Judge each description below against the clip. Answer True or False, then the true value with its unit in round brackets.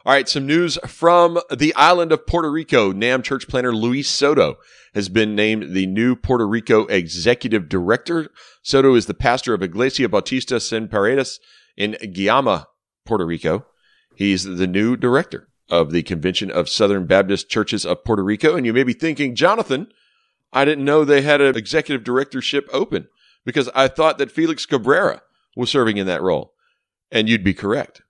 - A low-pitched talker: True (125 Hz)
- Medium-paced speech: True (175 wpm)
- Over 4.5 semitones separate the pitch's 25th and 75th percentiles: True (5.6 semitones)